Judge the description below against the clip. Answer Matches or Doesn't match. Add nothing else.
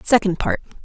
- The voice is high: Matches